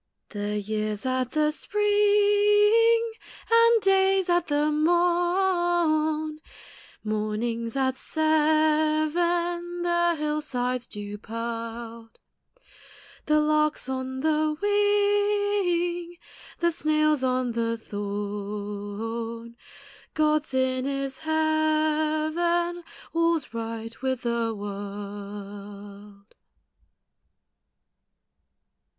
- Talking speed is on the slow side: Yes, slow, 75 wpm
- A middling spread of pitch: No, wide, 7.1 semitones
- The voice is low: No, very high, 305 Hz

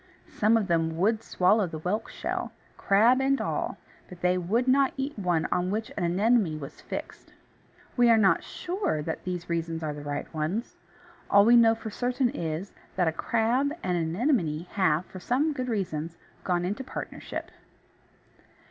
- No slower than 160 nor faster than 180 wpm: Yes, average, 175 wpm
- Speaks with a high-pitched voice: Yes, high, 195 Hz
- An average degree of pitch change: No, wide, 5.8 semitones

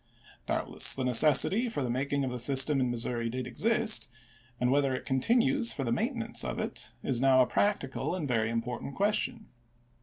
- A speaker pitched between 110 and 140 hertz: Yes, low, 135 Hz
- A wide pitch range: Yes, wide, 7.9 semitones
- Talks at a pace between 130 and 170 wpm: No, average, 180 wpm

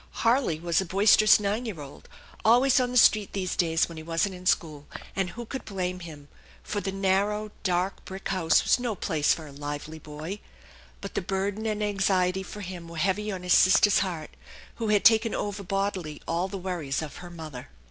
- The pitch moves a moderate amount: Yes, average, 3.8 semitones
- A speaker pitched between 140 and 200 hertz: Yes, high, 190 Hz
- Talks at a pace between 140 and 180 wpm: No, average, 200 wpm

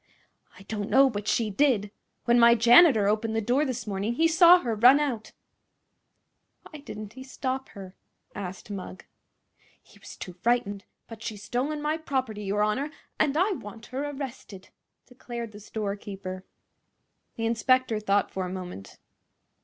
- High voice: Yes, high, 225 Hz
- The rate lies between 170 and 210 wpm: No, average, 155 wpm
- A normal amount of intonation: Yes, average, 4.4 semitones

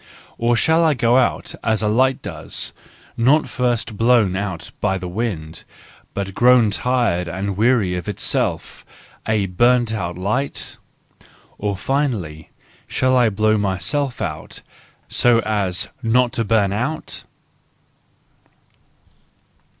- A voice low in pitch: Yes, low, 110 Hz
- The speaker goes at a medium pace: No, slow, 120 wpm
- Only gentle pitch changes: No, average, 4.4 semitones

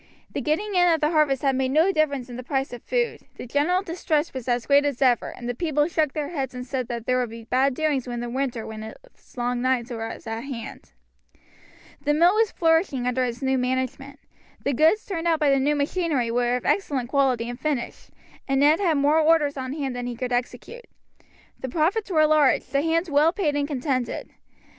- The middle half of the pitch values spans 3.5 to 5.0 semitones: Yes, average, 3.9 semitones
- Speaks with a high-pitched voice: Yes, very high, 275 Hz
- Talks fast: Yes, fast, 220 wpm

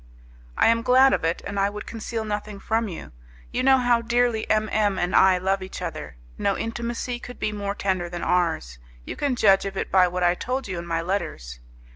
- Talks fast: Yes, fast, 220 wpm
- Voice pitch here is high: Yes, high, 200 Hz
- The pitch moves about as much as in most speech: Yes, average, 4.2 semitones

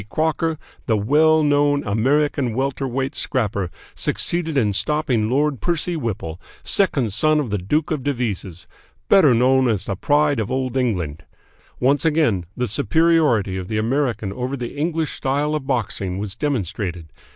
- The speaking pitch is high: No, low, 130 Hz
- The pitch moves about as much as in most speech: No, wide, 5.9 semitones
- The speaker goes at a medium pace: Yes, average, 150 wpm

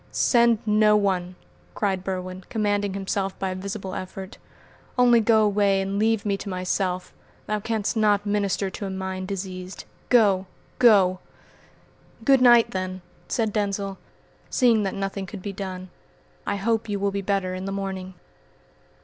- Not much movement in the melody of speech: Yes, narrow, 2.0 semitones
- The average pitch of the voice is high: Yes, high, 195 Hz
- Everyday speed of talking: Yes, average, 155 wpm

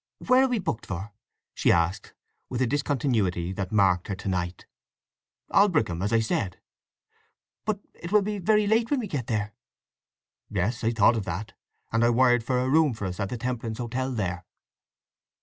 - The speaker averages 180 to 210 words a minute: Yes, average, 185 wpm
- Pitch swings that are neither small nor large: No, wide, 6.7 semitones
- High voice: No, low, 115 Hz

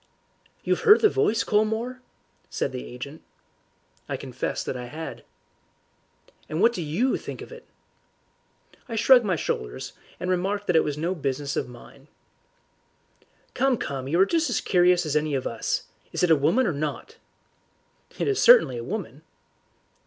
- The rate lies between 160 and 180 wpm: Yes, average, 165 wpm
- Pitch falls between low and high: Yes, medium, 180 Hz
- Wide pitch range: Yes, wide, 8.4 semitones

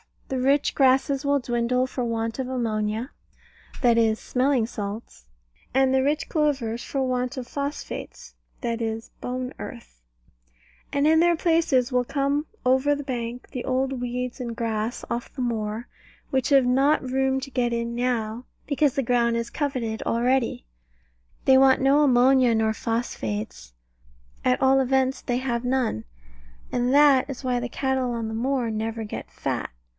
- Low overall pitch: No, very high, 250 Hz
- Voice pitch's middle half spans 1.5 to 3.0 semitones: Yes, narrow, 2.5 semitones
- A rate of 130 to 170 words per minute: Yes, average, 160 wpm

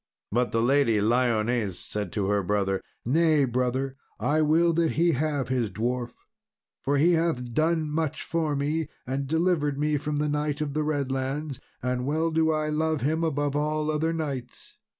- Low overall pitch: No, medium, 145 Hz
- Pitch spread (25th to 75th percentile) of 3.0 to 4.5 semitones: Yes, average, 3.9 semitones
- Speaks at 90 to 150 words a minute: No, average, 175 wpm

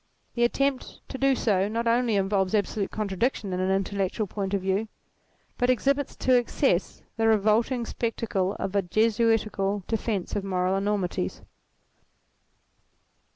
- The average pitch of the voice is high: Yes, high, 210 Hz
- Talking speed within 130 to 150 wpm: Yes, slow, 135 wpm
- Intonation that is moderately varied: Yes, average, 3.3 semitones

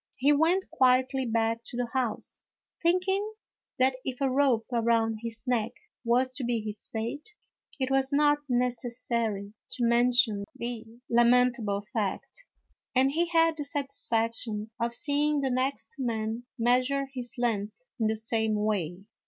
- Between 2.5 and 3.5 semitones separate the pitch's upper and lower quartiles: Yes, average, 3.2 semitones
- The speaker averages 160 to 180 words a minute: No, average, 145 wpm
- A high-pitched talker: Yes, high, 245 Hz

